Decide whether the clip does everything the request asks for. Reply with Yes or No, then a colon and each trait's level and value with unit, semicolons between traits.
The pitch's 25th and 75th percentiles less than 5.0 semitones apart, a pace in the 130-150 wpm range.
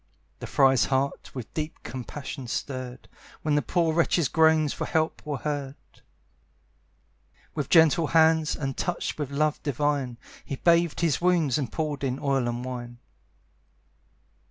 Yes: average, 3.2 semitones; average, 140 wpm